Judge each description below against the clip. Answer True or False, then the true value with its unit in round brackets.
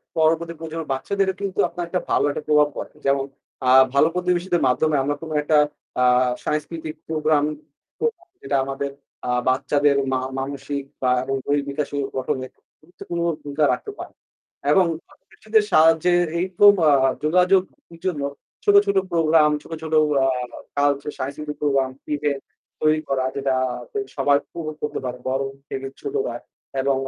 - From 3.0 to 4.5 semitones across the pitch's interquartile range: True (3.5 semitones)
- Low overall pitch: False (150 Hz)